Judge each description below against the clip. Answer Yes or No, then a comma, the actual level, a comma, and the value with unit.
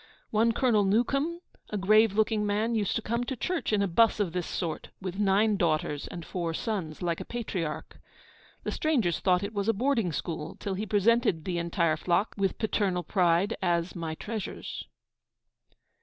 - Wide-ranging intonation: No, average, 4.3 semitones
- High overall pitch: Yes, high, 200 Hz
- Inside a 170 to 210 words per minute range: Yes, average, 175 wpm